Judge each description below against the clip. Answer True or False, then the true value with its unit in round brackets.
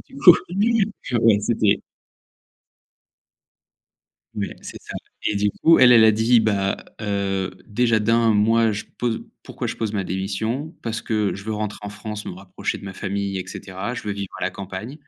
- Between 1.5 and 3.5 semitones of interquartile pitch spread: True (2.7 semitones)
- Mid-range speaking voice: False (105 Hz)